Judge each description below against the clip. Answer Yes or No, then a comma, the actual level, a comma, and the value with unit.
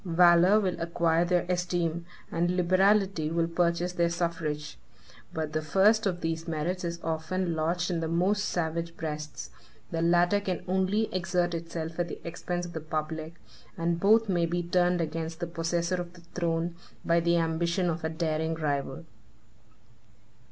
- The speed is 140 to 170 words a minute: Yes, average, 160 wpm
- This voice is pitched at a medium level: Yes, medium, 170 Hz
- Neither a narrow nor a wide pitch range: No, narrow, 1.5 semitones